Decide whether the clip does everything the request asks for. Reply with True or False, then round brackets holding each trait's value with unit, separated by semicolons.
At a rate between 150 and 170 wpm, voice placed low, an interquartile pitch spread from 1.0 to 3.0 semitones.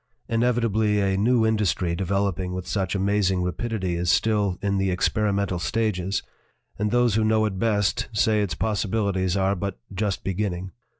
True (160 wpm; 100 Hz; 2.5 semitones)